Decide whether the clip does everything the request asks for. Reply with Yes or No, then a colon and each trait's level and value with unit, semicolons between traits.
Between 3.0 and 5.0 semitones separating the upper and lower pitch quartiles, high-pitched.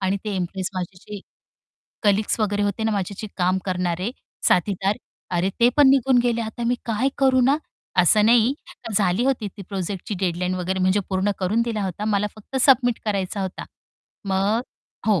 Yes: average, 3.3 semitones; high, 205 Hz